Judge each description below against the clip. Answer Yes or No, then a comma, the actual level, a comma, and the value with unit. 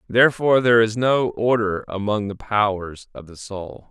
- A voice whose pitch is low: Yes, low, 110 Hz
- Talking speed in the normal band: Yes, average, 170 wpm